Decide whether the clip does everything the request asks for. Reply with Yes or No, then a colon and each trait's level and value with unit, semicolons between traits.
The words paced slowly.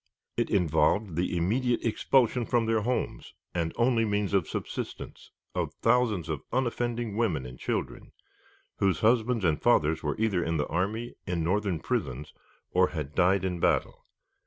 No: average, 155 wpm